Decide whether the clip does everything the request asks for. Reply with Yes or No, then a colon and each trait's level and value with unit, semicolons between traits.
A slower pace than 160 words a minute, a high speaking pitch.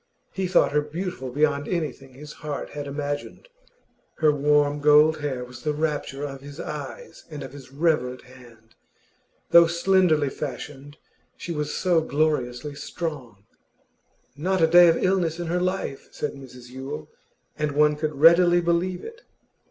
No: average, 150 wpm; medium, 150 Hz